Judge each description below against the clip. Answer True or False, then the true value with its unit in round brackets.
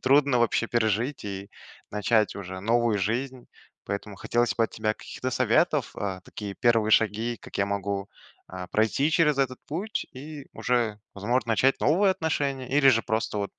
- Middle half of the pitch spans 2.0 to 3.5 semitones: False (4.4 semitones)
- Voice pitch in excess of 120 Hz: False (115 Hz)